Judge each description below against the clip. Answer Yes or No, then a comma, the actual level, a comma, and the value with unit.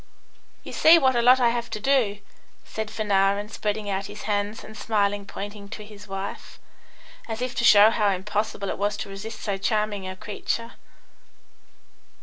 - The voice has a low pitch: No, high, 210 Hz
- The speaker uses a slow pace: No, average, 170 wpm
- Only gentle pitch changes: Yes, narrow, 1.8 semitones